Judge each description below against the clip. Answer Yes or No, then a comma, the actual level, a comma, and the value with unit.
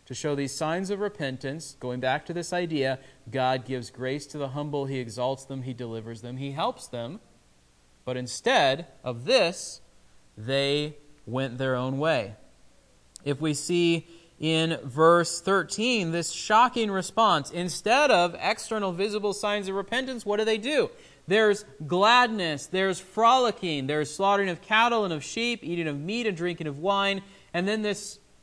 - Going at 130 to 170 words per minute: Yes, average, 160 wpm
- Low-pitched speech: No, medium, 160 Hz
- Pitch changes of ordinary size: No, wide, 7.0 semitones